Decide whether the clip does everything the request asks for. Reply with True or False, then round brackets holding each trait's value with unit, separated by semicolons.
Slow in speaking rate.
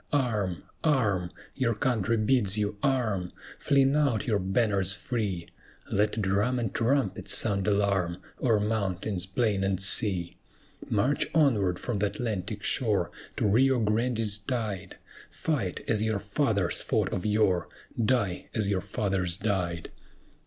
True (130 wpm)